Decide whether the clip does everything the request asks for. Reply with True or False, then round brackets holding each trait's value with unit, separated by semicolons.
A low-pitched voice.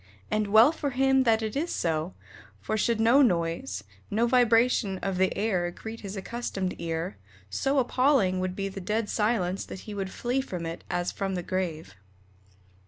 False (205 Hz)